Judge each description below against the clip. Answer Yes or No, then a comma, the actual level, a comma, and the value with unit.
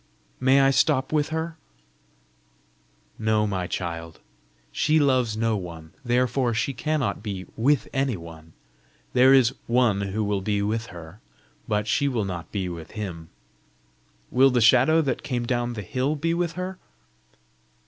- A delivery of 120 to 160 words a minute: Yes, average, 150 wpm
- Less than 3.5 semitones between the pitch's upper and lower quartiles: No, wide, 5.4 semitones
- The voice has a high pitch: No, low, 115 Hz